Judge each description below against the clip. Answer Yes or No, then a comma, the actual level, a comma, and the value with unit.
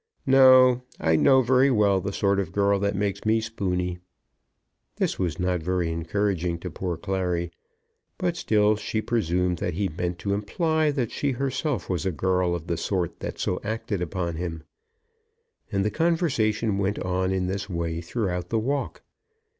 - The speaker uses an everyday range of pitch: Yes, average, 4.0 semitones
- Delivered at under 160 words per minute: No, average, 170 wpm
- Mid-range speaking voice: No, low, 100 Hz